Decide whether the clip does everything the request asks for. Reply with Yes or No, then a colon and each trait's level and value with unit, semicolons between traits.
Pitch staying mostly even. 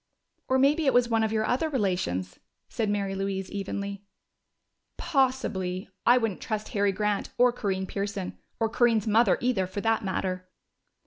No: average, 3.8 semitones